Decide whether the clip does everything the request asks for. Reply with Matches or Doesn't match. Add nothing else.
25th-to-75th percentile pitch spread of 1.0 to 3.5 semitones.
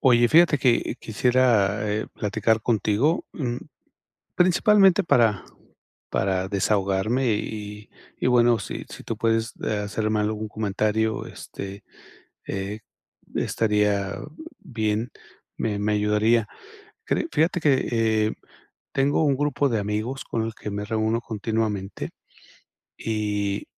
Matches